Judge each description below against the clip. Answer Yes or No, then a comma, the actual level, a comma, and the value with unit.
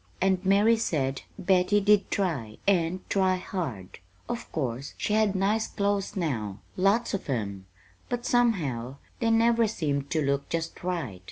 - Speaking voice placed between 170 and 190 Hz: Yes, medium, 185 Hz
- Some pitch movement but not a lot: No, wide, 6.7 semitones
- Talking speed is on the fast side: No, average, 150 wpm